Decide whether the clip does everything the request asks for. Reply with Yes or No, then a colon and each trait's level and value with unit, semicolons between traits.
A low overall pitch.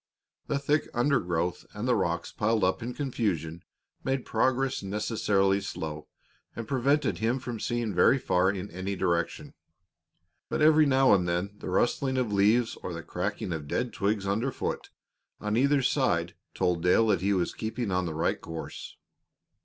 Yes: low, 105 Hz